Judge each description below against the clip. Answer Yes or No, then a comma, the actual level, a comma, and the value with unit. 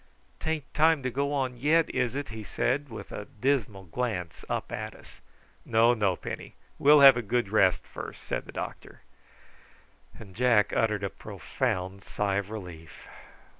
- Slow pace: No, average, 165 wpm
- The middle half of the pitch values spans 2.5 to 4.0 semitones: No, wide, 5.5 semitones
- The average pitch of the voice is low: Yes, low, 115 Hz